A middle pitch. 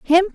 No: very high, 365 Hz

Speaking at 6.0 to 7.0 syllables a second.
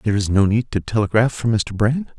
Yes: 6.2 syllables/s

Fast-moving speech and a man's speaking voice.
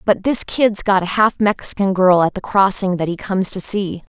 No: fast, 230 wpm; female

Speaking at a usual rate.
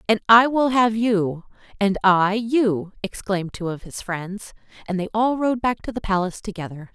Yes: average, 190 wpm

